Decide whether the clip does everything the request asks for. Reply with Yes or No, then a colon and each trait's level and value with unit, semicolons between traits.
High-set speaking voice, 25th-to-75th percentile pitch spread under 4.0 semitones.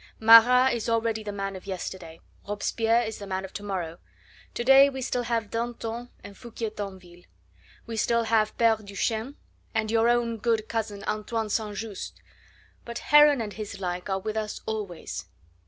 Yes: high, 220 Hz; narrow, 2.5 semitones